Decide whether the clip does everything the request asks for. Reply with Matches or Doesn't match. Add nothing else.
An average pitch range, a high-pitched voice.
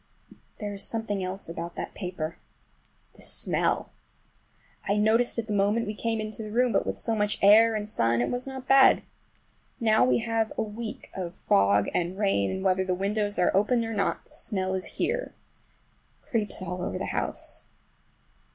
Matches